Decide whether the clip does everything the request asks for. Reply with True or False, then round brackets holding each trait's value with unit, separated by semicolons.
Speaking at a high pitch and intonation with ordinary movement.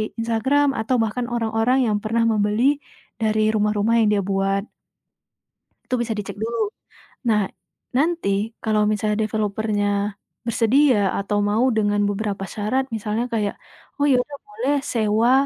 False (220 Hz; 2.3 semitones)